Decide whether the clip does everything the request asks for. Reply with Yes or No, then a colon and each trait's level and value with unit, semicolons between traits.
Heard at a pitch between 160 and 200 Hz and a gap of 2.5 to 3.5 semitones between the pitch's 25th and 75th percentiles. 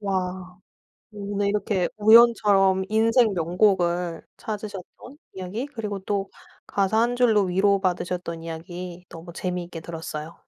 Yes: high, 190 Hz; average, 3.0 semitones